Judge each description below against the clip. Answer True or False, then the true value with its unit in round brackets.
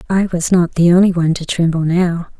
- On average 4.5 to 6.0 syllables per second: True (5.9 syllables/s)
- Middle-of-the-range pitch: True (175 Hz)